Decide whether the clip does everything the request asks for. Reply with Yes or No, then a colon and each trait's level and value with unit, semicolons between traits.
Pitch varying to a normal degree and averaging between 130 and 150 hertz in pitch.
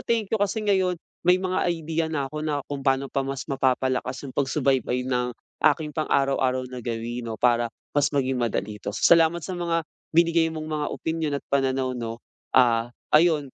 Yes: average, 4.3 semitones; medium, 140 Hz